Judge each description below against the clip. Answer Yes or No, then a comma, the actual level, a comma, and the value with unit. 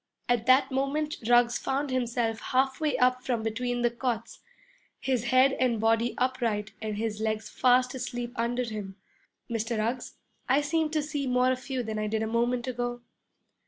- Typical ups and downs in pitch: No, narrow, 2.3 semitones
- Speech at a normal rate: Yes, average, 170 wpm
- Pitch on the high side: Yes, high, 245 Hz